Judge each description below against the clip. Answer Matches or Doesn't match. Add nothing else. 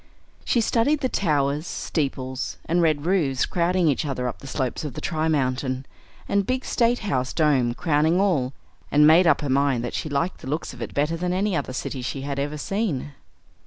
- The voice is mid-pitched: Matches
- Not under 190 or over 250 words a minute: Matches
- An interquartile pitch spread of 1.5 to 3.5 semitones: Doesn't match